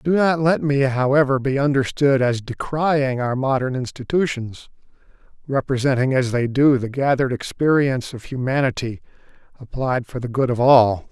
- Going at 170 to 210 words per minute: No, average, 145 wpm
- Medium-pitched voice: No, low, 130 Hz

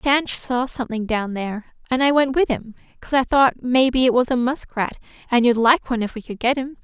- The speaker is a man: No, female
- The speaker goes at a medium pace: No, fast, 255 wpm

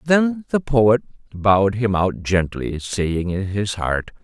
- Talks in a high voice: No, low, 105 Hz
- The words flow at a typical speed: Yes, average, 155 wpm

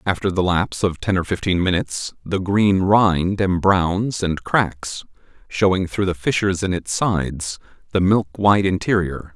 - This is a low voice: Yes, very low, 95 Hz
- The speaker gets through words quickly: No, average, 160 wpm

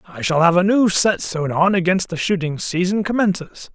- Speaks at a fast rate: Yes, fast, 210 wpm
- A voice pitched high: No, medium, 180 Hz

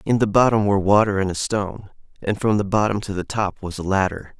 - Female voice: No, male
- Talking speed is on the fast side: Yes, fast, 245 wpm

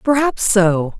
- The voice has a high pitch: Yes, high, 215 Hz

